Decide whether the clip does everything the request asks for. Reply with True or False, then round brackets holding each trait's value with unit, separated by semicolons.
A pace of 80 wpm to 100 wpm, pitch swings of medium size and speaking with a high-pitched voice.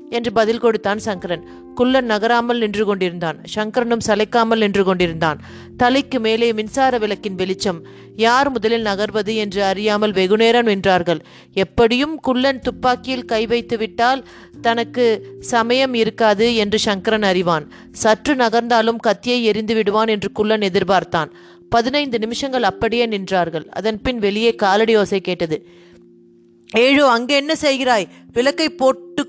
False (120 wpm; 3.5 semitones; 220 Hz)